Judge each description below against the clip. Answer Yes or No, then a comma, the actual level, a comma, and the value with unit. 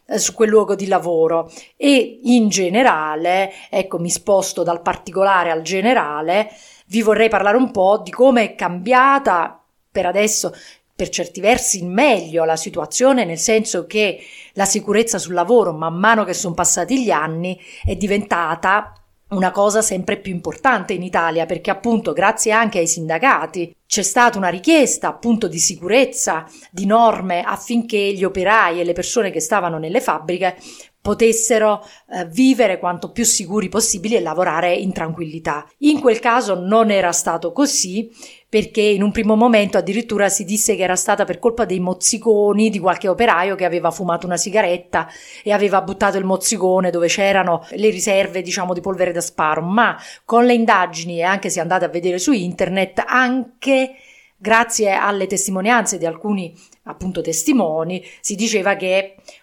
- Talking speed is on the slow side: No, average, 160 wpm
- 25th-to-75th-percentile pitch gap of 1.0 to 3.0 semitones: No, average, 4.0 semitones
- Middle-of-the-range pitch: No, high, 195 Hz